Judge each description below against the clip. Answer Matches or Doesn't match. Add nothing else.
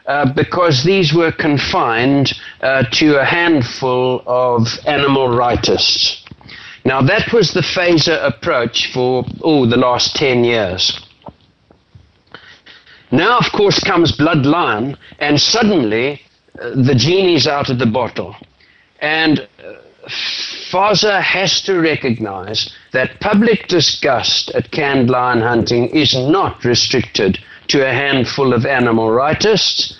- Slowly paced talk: Matches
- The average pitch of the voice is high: Doesn't match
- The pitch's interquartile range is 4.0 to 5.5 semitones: Matches